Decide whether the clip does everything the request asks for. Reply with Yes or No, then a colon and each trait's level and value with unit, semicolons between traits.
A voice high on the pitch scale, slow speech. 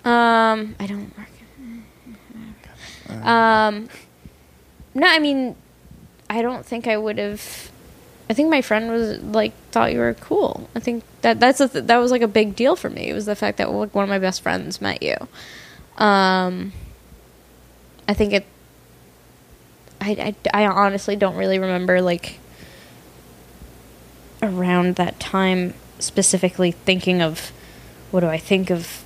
No: high, 195 Hz; average, 155 wpm